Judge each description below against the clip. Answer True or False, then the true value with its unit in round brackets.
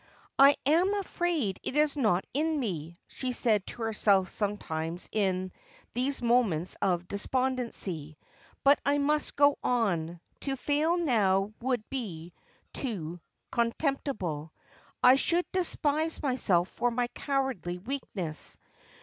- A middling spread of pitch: False (7.2 semitones)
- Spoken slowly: True (125 wpm)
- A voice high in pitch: True (235 Hz)